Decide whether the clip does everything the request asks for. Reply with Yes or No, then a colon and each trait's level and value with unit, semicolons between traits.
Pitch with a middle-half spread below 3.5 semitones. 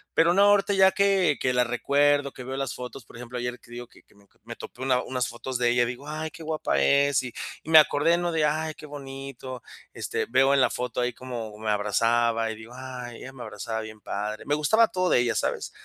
No: average, 3.8 semitones